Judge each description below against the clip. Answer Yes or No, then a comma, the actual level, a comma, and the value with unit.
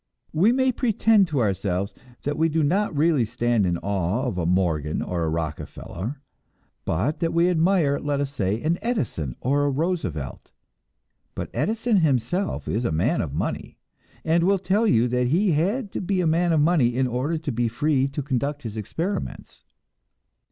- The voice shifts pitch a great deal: Yes, wide, 7.6 semitones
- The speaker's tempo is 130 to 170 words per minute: No, average, 180 wpm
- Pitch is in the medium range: Yes, medium, 145 Hz